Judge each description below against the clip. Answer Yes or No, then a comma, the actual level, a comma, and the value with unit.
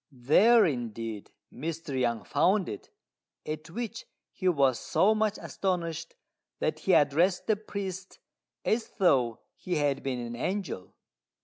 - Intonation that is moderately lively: No, wide, 7.1 semitones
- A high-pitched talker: No, medium, 165 Hz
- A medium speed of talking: No, slow, 130 wpm